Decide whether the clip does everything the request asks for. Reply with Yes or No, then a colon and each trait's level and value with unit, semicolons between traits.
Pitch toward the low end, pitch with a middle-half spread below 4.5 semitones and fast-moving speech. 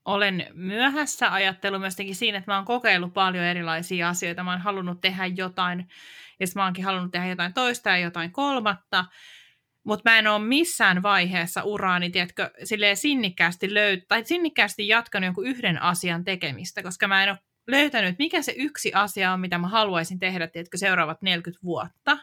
No: high, 190 Hz; average, 2.9 semitones; fast, 160 wpm